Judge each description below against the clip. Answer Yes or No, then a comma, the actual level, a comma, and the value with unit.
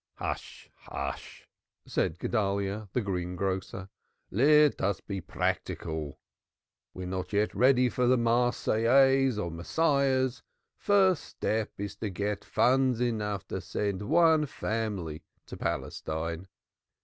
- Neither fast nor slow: No, slow, 115 wpm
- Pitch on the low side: Yes, low, 105 Hz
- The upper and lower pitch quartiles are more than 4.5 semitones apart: Yes, wide, 5.6 semitones